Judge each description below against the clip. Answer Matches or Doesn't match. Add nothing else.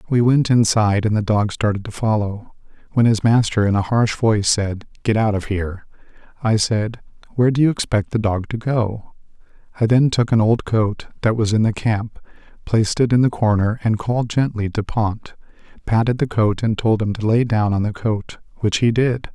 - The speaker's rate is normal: Doesn't match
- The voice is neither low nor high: Doesn't match